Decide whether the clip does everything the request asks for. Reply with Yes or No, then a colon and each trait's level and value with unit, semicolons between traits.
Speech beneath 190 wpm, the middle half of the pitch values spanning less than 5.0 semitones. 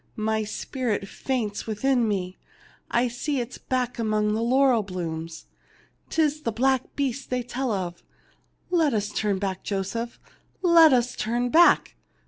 Yes: average, 140 wpm; average, 4.1 semitones